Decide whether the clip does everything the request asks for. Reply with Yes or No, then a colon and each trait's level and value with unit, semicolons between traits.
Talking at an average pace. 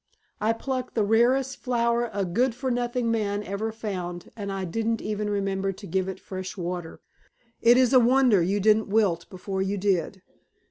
Yes: average, 180 wpm